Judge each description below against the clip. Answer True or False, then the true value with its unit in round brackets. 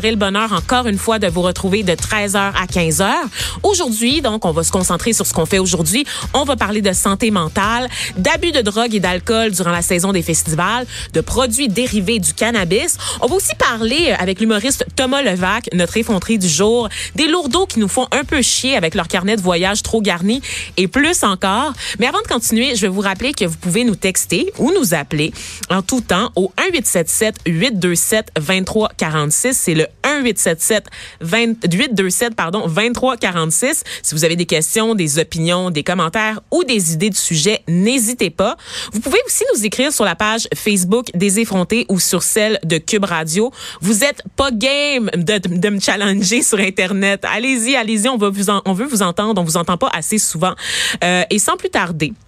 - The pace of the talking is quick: False (190 wpm)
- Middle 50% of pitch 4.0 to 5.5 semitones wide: True (4.7 semitones)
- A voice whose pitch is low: False (210 Hz)